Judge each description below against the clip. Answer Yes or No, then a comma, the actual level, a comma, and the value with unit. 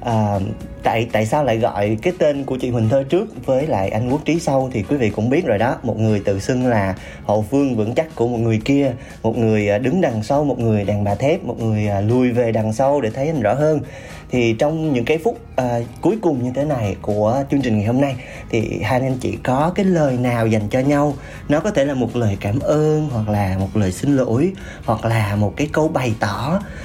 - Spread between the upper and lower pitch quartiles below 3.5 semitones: No, average, 4.5 semitones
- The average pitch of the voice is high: No, low, 125 Hz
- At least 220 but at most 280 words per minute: Yes, average, 245 wpm